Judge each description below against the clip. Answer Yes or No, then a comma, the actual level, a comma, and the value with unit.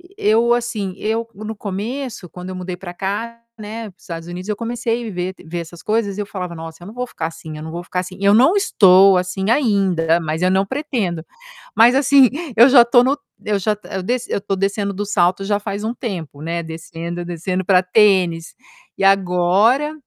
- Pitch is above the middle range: Yes, high, 195 Hz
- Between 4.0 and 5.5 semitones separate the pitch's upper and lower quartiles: Yes, average, 4.3 semitones